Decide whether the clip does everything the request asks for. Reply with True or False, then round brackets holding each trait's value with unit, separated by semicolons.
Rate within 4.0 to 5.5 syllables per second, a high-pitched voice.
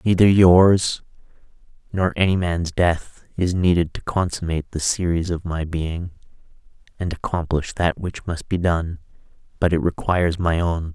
False (4.5 syllables/s; 85 Hz)